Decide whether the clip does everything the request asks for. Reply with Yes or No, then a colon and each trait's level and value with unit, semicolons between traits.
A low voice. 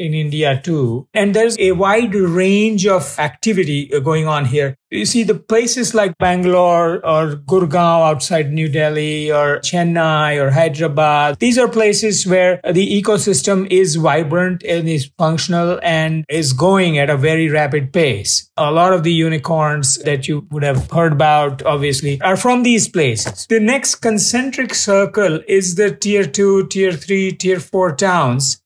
No: medium, 170 Hz